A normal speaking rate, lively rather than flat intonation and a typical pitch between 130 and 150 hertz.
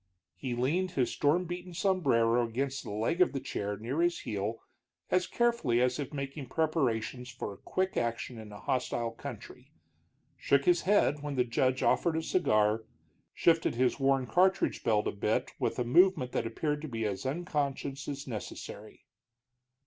Yes: average, 165 wpm; wide, 5.7 semitones; low, 135 Hz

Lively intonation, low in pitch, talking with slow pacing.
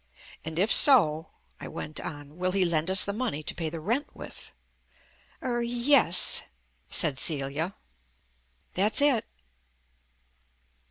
No: wide, 7.2 semitones; medium, 185 Hz; slow, 125 wpm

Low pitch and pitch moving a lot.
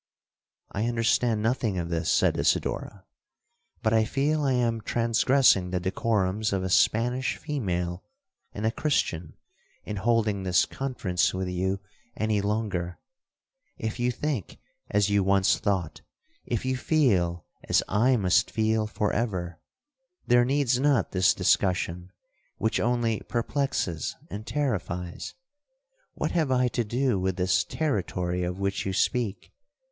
No: low, 110 Hz; average, 4.8 semitones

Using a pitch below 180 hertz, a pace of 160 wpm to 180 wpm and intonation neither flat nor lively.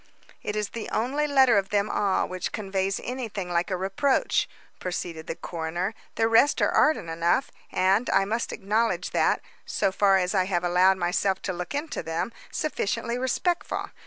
No: high, 195 Hz; average, 170 wpm; average, 4.2 semitones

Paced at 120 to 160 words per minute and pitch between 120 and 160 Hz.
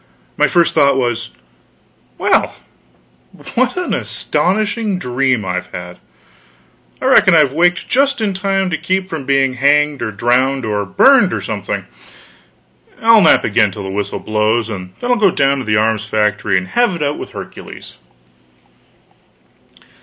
Yes: average, 155 wpm; low, 135 Hz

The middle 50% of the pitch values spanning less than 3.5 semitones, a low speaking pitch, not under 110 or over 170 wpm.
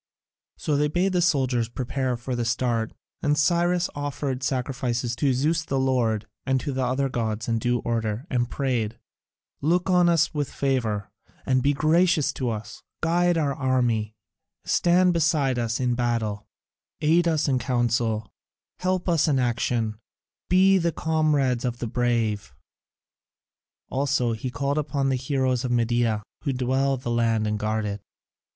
No: average, 4.0 semitones; low, 130 Hz; average, 160 wpm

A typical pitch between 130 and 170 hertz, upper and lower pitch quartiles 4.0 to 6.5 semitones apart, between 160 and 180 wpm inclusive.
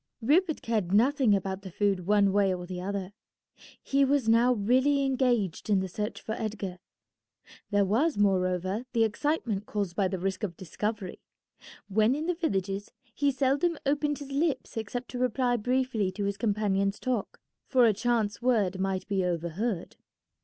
No: high, 210 Hz; average, 4.7 semitones; average, 165 wpm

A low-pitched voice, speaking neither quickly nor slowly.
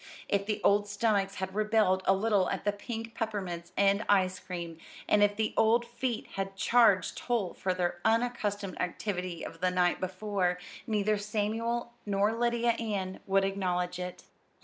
No: high, 200 Hz; average, 160 wpm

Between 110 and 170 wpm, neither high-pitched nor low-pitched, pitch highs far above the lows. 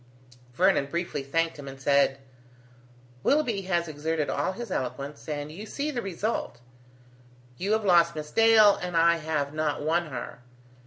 No: average, 155 wpm; medium, 165 Hz; average, 5.0 semitones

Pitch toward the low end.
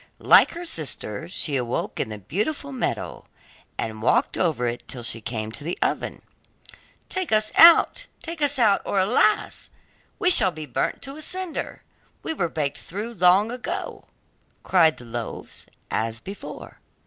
No: medium, 180 Hz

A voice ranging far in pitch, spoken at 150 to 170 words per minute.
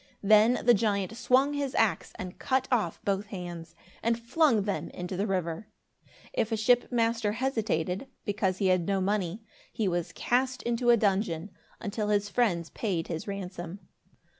No: average, 4.1 semitones; average, 165 wpm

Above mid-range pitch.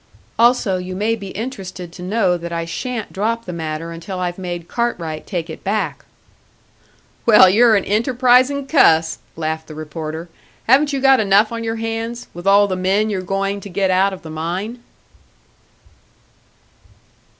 Yes: high, 195 Hz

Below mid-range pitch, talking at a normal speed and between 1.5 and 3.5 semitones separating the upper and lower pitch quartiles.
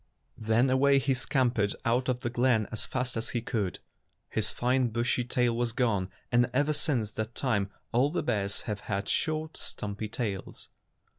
Yes: low, 120 Hz; average, 180 wpm; average, 3.0 semitones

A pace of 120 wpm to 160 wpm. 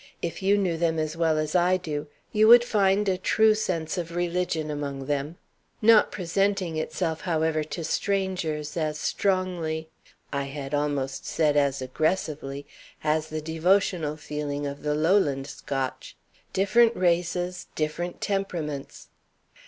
Yes: slow, 135 wpm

